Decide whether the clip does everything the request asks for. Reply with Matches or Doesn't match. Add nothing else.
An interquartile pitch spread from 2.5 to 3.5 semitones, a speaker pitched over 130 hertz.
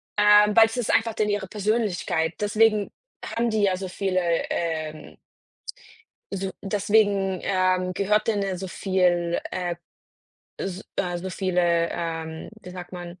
Matches